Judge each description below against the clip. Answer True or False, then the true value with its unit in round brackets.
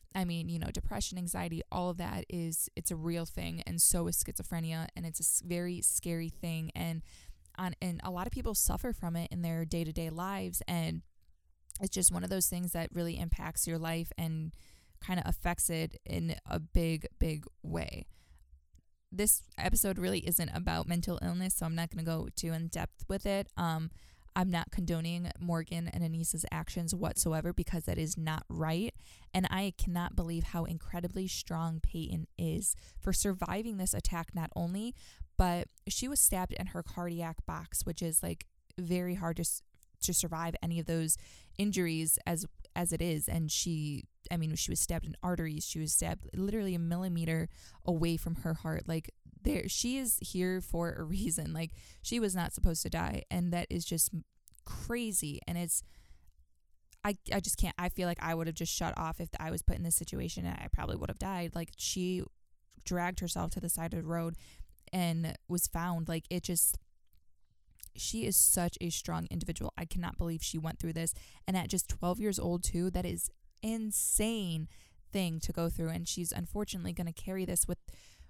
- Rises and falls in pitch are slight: True (2.3 semitones)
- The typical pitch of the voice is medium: True (170 Hz)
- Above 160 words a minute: True (190 wpm)